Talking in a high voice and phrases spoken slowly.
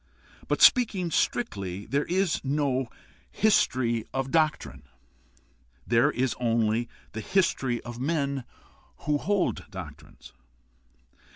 No: low, 135 Hz; slow, 100 wpm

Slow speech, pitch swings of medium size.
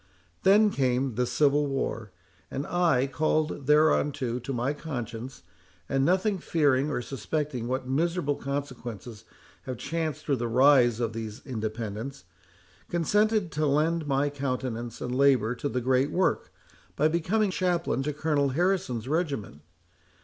Yes: slow, 130 wpm; average, 4.2 semitones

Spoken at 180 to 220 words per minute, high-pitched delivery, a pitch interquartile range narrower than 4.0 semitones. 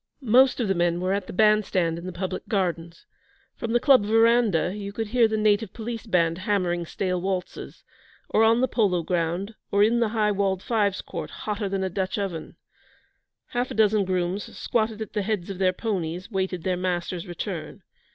Yes: average, 190 wpm; high, 195 Hz; average, 3.3 semitones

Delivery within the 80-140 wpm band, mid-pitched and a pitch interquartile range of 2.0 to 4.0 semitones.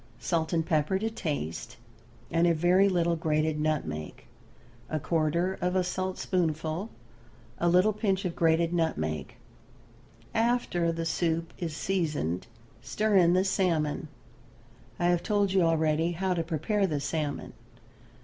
Yes: slow, 135 wpm; medium, 170 Hz; average, 3.1 semitones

